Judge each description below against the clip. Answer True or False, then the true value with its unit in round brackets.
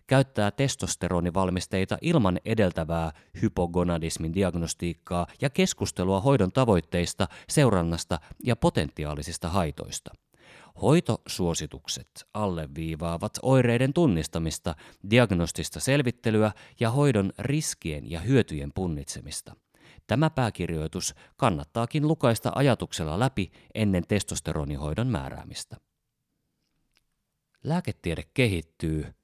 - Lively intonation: True (6.6 semitones)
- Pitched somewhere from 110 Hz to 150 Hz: False (95 Hz)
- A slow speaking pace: True (75 wpm)